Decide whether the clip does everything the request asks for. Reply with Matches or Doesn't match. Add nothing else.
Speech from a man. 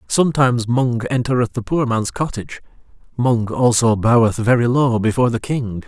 Matches